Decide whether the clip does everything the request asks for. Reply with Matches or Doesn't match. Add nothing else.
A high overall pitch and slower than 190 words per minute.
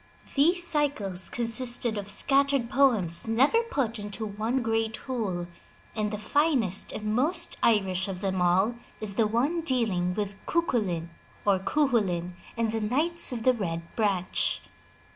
Matches